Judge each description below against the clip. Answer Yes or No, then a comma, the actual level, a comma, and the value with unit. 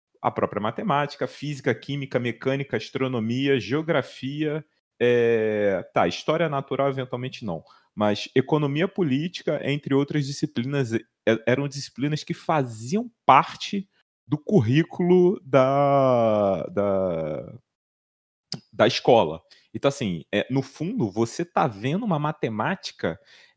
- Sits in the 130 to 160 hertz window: Yes, medium, 140 Hz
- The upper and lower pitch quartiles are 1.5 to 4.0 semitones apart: No, average, 4.5 semitones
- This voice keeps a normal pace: No, slow, 105 wpm